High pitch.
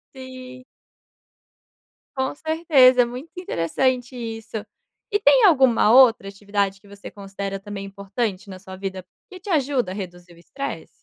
Yes: high, 225 Hz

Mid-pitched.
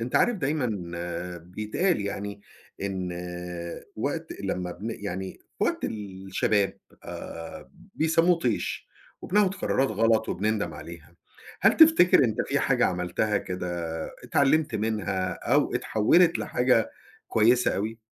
No: low, 110 Hz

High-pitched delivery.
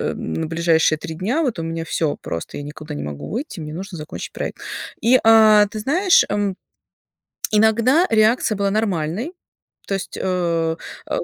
Yes: high, 195 Hz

